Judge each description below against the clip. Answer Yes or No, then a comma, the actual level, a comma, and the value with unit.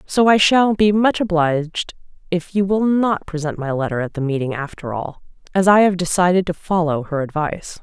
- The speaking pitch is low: No, medium, 175 Hz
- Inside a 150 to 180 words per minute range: No, average, 200 wpm